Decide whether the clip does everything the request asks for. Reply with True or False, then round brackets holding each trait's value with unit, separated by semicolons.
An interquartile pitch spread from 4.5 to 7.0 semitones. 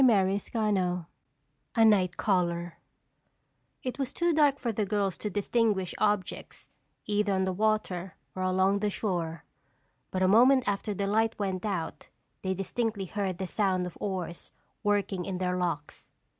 False (2.6 semitones)